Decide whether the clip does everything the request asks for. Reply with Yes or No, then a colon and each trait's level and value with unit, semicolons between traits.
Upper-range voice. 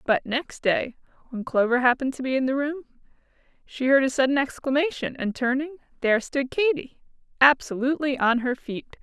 Yes: very high, 265 Hz